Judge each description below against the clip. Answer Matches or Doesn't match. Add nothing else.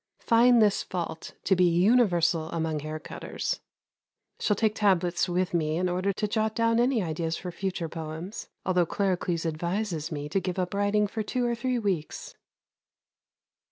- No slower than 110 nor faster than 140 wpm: Doesn't match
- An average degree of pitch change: Matches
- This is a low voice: Doesn't match